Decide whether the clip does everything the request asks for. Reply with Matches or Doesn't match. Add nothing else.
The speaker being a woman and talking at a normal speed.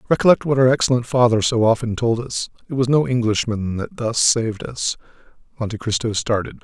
Doesn't match